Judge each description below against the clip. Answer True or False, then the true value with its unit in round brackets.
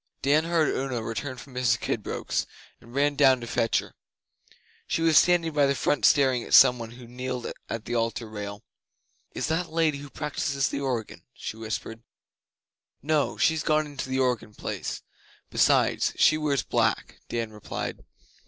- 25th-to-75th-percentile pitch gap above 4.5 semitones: False (4.2 semitones)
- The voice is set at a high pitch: False (130 Hz)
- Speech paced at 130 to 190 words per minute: True (170 wpm)